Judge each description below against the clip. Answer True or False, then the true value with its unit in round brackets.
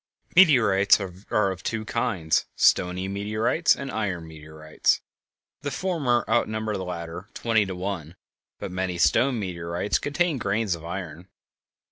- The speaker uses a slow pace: True (130 wpm)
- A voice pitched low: True (100 Hz)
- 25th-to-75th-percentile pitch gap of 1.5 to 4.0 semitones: False (4.5 semitones)